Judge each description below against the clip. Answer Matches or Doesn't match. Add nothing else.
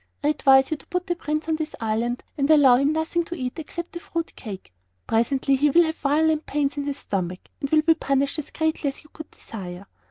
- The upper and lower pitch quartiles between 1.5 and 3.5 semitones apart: Matches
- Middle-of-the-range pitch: Doesn't match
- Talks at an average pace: Doesn't match